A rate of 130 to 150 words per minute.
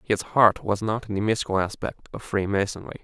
No: average, 200 wpm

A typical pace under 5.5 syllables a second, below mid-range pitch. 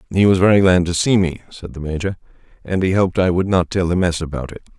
No: 6.5 syllables/s; very low, 90 Hz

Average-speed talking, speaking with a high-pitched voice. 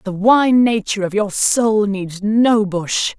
Yes: average, 170 wpm; high, 210 Hz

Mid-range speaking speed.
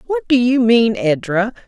Yes: average, 180 wpm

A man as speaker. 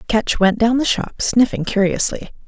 No: female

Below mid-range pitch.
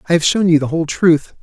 No: medium, 165 Hz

